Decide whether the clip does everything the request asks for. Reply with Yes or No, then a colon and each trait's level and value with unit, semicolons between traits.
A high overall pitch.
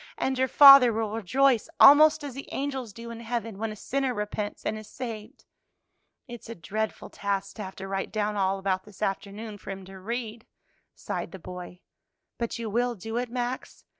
Yes: high, 220 Hz